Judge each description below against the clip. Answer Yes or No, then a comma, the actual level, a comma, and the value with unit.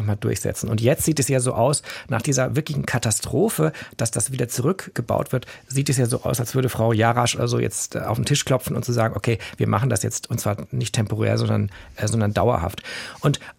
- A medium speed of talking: No, fast, 225 wpm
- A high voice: No, low, 120 Hz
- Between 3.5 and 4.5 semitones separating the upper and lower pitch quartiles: No, average, 2.8 semitones